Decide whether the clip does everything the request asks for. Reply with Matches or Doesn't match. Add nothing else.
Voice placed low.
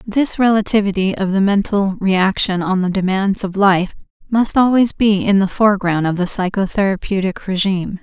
Doesn't match